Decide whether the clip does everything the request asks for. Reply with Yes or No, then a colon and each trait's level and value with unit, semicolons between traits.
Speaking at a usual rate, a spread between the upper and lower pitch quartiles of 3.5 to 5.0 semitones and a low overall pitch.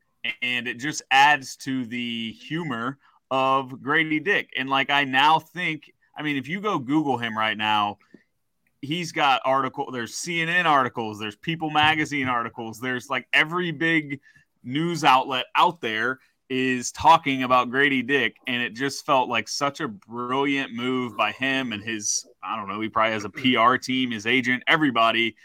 Yes: average, 170 wpm; average, 3.9 semitones; low, 130 Hz